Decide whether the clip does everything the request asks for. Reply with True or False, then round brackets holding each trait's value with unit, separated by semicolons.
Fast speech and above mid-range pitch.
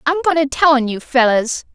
True (240 wpm; 265 Hz)